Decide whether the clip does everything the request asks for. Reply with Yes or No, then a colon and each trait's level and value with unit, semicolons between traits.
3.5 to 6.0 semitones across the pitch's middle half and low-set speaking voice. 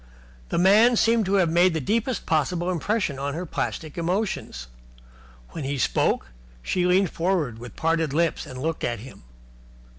No: average, 5.0 semitones; medium, 170 Hz